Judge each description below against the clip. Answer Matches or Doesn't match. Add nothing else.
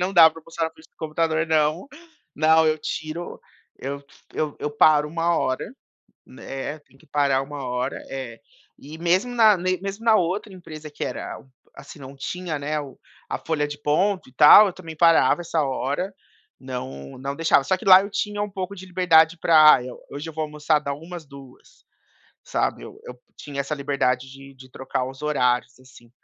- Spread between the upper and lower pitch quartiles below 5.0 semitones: Matches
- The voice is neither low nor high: Matches